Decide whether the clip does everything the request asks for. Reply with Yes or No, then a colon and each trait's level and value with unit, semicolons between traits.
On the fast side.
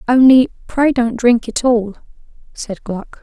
No: average, 150 wpm